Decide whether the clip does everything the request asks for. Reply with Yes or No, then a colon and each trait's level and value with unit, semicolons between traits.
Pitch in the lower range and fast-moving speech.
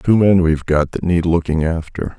Yes: very low, 85 Hz; fast, 220 wpm